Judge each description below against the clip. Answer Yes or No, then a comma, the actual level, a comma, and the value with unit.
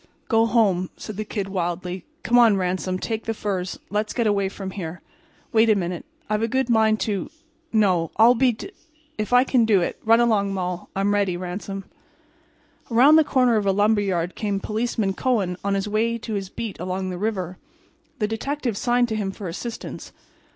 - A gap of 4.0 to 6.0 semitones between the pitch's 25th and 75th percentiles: No, average, 3.4 semitones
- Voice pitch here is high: Yes, high, 210 Hz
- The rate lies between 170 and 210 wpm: Yes, average, 180 wpm